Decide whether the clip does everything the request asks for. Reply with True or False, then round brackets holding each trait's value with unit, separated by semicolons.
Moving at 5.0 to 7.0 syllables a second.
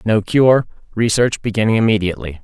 True (5.8 syllables/s)